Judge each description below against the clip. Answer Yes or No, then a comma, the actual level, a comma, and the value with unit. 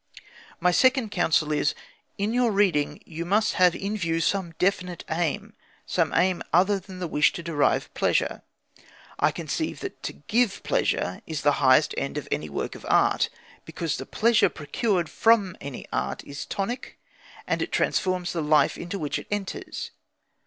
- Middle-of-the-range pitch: Yes, medium, 175 Hz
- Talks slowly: No, average, 165 wpm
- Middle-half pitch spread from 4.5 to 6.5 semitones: Yes, average, 4.9 semitones